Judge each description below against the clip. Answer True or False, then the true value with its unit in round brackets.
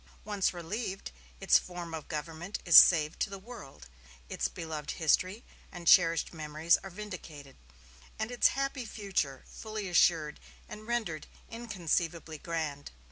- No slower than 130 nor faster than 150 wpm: True (135 wpm)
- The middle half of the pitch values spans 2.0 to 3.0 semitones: False (4.8 semitones)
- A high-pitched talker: False (175 Hz)